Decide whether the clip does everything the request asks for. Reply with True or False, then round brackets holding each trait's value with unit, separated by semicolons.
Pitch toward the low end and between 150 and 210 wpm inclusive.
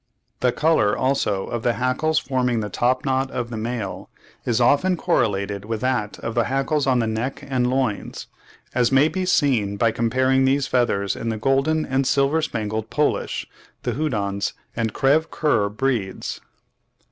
True (125 Hz; 165 wpm)